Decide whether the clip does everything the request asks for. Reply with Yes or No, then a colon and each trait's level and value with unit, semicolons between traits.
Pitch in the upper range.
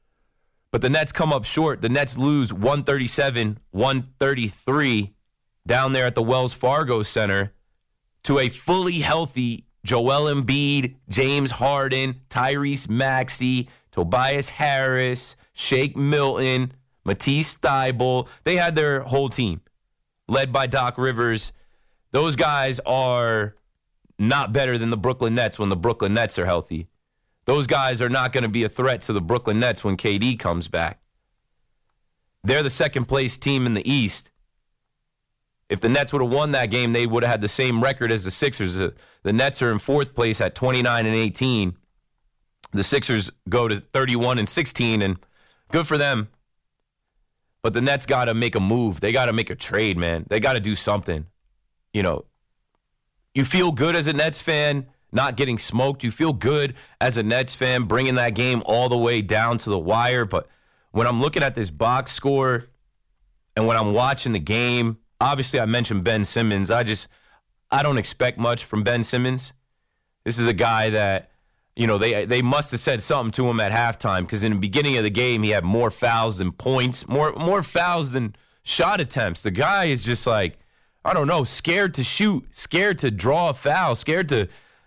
No: low, 125 Hz